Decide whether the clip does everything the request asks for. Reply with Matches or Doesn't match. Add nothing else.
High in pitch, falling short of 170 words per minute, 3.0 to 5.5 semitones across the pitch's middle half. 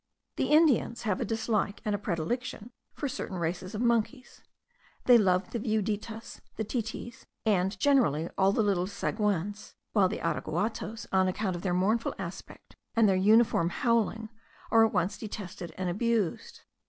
Matches